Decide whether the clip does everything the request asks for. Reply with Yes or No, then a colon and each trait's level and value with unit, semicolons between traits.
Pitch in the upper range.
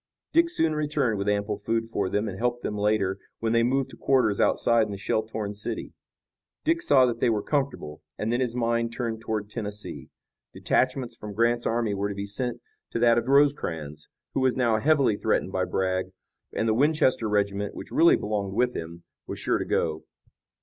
No: low, 115 Hz